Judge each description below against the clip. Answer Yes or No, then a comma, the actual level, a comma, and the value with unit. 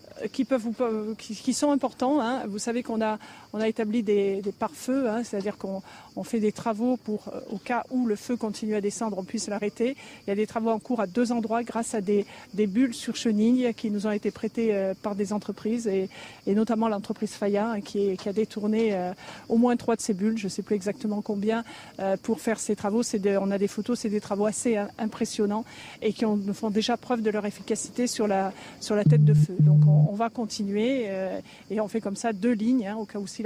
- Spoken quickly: Yes, fast, 240 wpm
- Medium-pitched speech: No, high, 220 Hz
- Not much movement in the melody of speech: Yes, narrow, 2.1 semitones